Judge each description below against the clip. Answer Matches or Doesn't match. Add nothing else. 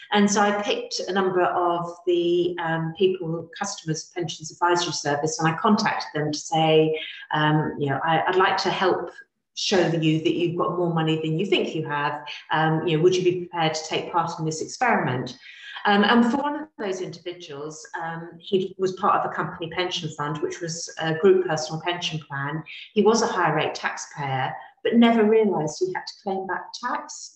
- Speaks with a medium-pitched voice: Matches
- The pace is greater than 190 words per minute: Matches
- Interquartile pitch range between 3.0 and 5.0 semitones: Matches